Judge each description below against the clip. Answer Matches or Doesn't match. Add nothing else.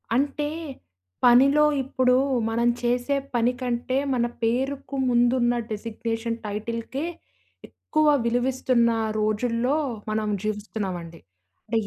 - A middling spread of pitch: Doesn't match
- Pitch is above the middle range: Matches